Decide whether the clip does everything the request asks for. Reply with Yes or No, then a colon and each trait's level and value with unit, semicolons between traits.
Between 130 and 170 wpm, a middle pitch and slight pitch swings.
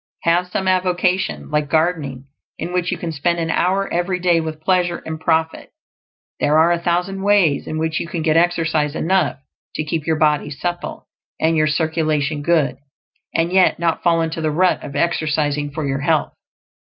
No: average, 180 wpm; medium, 165 Hz; narrow, 2.3 semitones